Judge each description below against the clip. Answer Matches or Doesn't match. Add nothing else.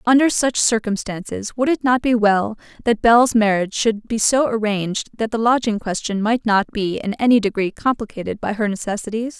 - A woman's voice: Matches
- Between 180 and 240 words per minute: Matches